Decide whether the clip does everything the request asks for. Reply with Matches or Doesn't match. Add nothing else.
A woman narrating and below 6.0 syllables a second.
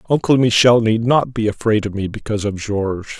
Doesn't match